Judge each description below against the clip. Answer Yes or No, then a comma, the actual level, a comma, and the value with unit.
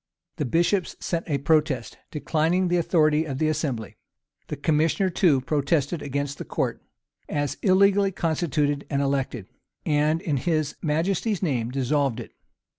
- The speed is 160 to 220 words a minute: No, average, 145 wpm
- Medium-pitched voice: Yes, medium, 150 Hz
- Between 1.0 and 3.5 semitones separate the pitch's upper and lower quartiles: Yes, average, 3.2 semitones